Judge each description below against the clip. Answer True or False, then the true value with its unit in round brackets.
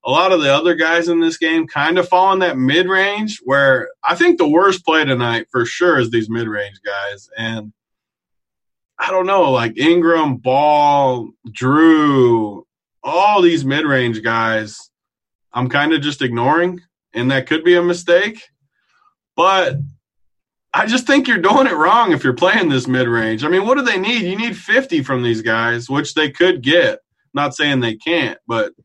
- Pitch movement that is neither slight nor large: False (7.1 semitones)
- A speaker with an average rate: True (185 wpm)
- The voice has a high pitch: False (150 Hz)